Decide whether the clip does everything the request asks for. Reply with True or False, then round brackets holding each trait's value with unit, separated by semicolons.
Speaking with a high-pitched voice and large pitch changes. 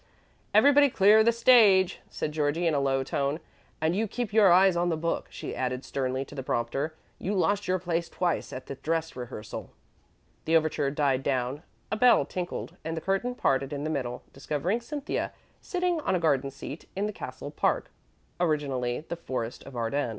False (160 Hz; 5.9 semitones)